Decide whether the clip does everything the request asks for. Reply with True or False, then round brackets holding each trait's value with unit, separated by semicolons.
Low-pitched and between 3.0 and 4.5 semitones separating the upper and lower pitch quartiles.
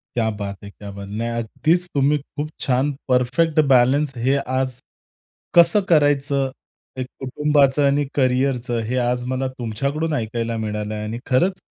True (130 Hz; 3.6 semitones)